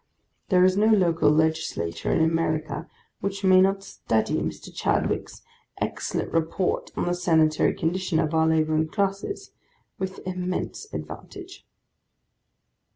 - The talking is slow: Yes, slow, 120 wpm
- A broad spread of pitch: No, average, 3.3 semitones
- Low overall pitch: No, medium, 175 Hz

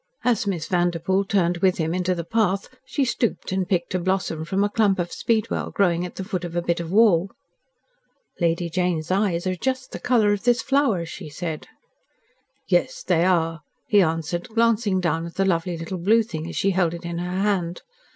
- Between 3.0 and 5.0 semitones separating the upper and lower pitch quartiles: Yes, average, 3.3 semitones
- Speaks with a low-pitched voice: No, medium, 185 Hz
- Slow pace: No, average, 200 wpm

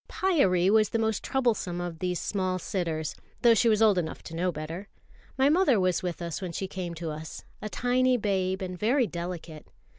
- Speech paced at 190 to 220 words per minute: Yes, average, 200 wpm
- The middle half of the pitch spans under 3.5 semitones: No, average, 4.4 semitones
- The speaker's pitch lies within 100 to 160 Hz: No, medium, 185 Hz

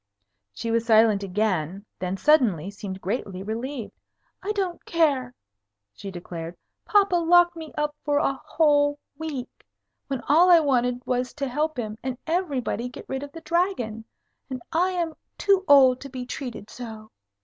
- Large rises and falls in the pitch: Yes, wide, 6.4 semitones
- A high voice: Yes, very high, 260 Hz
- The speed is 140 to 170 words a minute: Yes, average, 160 wpm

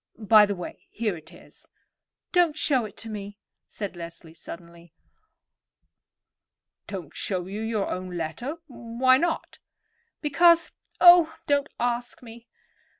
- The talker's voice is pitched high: Yes, high, 220 Hz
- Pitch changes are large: Yes, wide, 7.1 semitones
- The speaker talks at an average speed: No, slow, 120 wpm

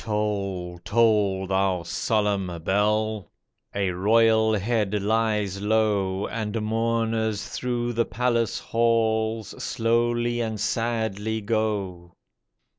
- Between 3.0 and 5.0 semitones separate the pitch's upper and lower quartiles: No, narrow, 2.4 semitones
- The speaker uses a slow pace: Yes, slow, 95 wpm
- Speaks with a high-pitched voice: No, low, 110 Hz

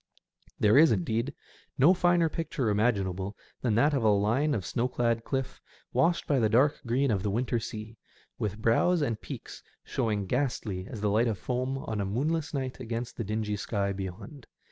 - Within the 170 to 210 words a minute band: Yes, average, 185 wpm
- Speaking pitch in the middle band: No, low, 115 Hz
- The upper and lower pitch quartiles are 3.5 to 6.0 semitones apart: Yes, average, 4.4 semitones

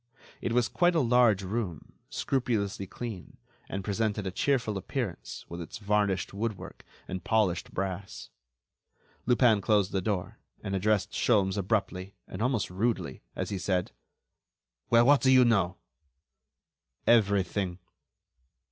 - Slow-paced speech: Yes, slow, 130 wpm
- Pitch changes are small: No, average, 3.6 semitones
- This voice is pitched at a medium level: No, low, 100 Hz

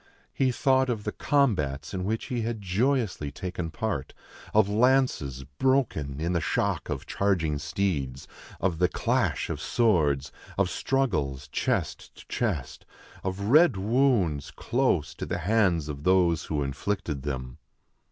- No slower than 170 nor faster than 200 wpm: No, average, 140 wpm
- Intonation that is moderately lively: No, wide, 7.9 semitones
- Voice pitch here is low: Yes, very low, 95 Hz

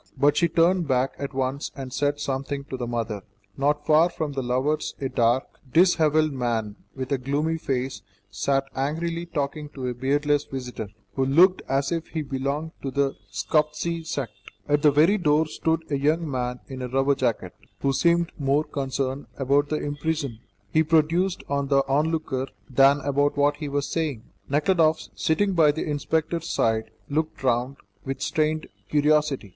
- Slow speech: No, average, 170 wpm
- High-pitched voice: No, medium, 145 Hz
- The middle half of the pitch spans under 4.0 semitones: Yes, average, 2.8 semitones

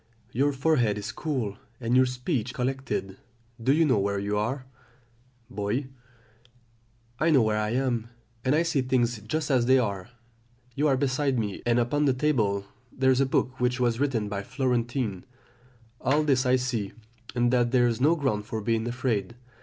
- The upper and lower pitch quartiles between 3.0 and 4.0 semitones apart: Yes, average, 3.3 semitones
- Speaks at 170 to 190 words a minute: Yes, average, 180 wpm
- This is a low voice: Yes, low, 125 Hz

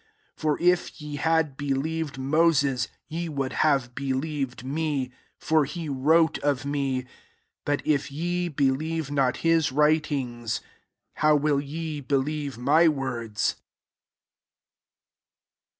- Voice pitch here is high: No, medium, 145 Hz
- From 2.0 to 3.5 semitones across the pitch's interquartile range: Yes, average, 2.8 semitones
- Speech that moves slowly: Yes, slow, 120 wpm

